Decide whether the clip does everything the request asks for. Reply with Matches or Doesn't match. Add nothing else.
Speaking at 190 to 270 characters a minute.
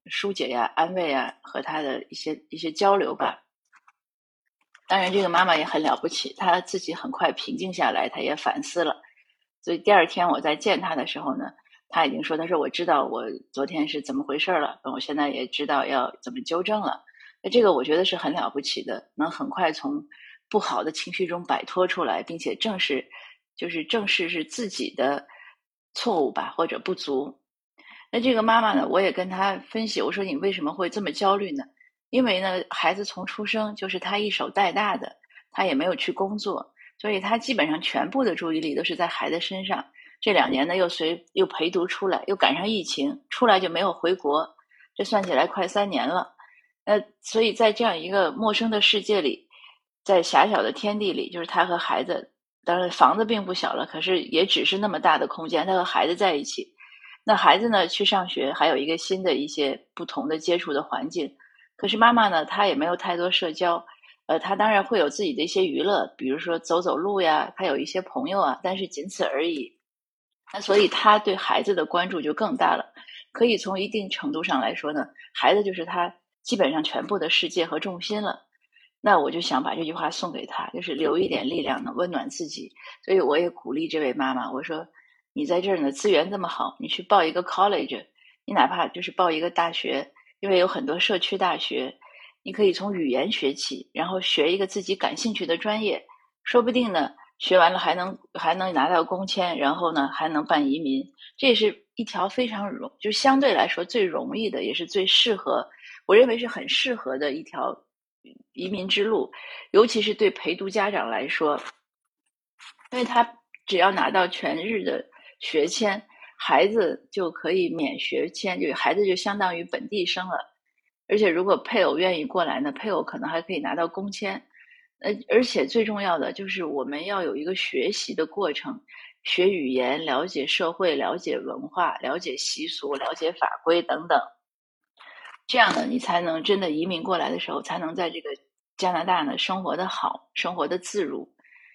Doesn't match